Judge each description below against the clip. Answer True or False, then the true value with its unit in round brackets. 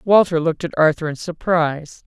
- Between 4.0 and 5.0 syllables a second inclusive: False (5.6 syllables/s)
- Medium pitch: True (165 Hz)